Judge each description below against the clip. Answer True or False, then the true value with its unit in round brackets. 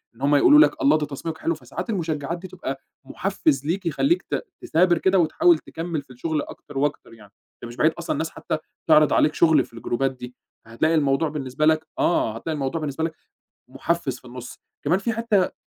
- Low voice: False (155 Hz)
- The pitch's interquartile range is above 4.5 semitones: False (4.0 semitones)